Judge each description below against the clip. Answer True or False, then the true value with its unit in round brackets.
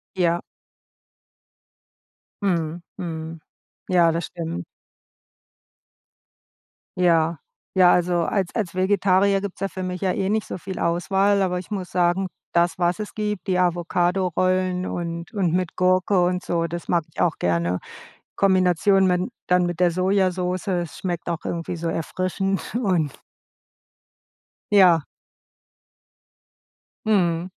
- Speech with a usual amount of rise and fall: False (1.8 semitones)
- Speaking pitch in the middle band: True (180 Hz)